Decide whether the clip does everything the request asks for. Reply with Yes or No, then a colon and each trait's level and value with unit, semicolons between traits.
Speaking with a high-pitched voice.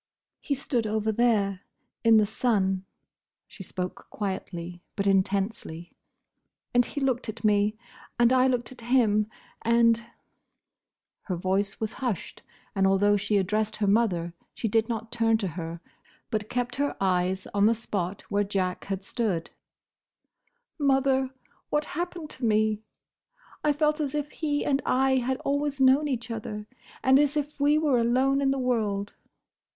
Yes: high, 225 Hz